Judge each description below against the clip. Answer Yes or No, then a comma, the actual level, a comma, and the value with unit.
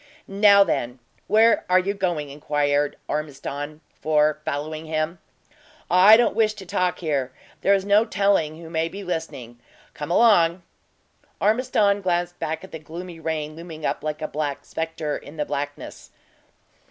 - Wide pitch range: No, average, 4.2 semitones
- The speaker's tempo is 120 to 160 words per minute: Yes, average, 155 wpm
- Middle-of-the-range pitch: Yes, medium, 160 Hz